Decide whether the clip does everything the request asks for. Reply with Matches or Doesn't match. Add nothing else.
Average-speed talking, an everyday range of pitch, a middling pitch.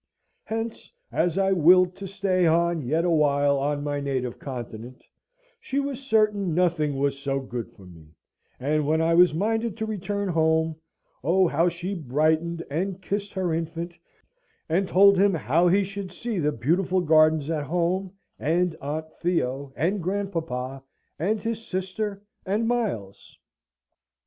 Matches